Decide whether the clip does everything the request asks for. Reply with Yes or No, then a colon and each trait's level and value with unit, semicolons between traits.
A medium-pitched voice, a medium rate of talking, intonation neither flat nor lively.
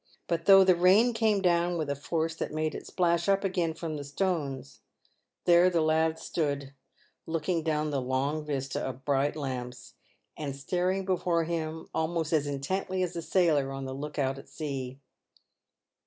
Yes: medium, 160 Hz; average, 170 wpm; average, 3.8 semitones